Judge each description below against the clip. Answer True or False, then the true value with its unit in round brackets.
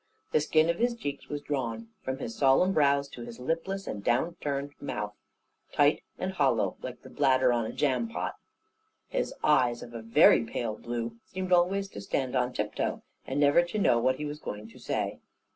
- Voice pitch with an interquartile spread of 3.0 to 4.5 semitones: False (5.0 semitones)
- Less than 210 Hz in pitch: True (135 Hz)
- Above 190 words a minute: True (200 wpm)